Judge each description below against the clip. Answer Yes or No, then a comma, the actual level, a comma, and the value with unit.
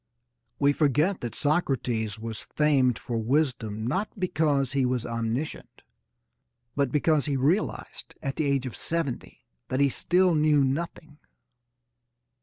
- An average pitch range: Yes, average, 3.8 semitones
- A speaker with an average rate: No, slow, 130 wpm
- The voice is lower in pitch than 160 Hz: Yes, medium, 140 Hz